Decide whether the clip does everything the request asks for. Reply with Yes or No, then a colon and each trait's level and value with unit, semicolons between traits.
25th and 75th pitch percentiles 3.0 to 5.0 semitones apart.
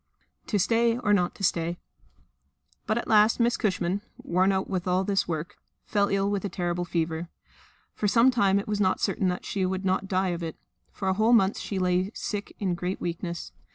No: narrow, 2.4 semitones